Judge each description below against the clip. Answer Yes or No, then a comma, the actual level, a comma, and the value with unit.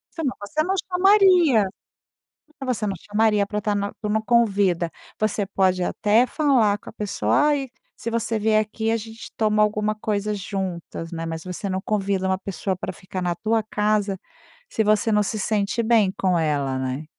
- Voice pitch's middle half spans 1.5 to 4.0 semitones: Yes, average, 2.7 semitones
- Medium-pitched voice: No, high, 210 Hz